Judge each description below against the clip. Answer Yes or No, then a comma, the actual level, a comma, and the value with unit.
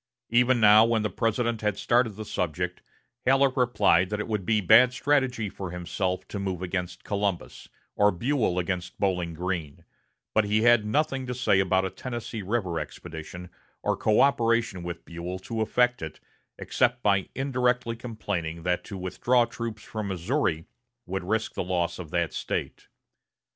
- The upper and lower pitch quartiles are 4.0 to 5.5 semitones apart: Yes, average, 4.8 semitones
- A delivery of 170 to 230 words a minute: No, average, 160 wpm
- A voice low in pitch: Yes, low, 105 Hz